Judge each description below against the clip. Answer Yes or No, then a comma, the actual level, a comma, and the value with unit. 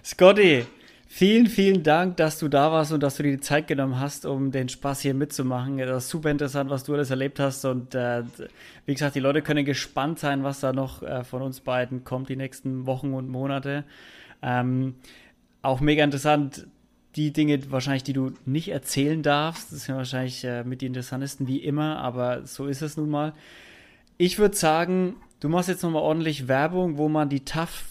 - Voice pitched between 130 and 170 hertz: Yes, medium, 140 Hz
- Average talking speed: No, fast, 200 wpm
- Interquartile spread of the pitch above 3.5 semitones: No, narrow, 2.5 semitones